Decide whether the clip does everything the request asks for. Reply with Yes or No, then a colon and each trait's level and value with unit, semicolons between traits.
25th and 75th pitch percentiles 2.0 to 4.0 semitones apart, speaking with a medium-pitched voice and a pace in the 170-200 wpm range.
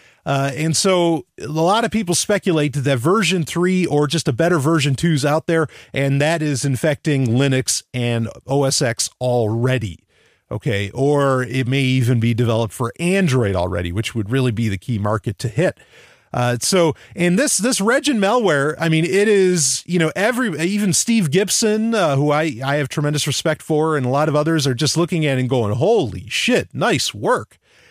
No: average, 5.3 semitones; medium, 150 Hz; average, 190 wpm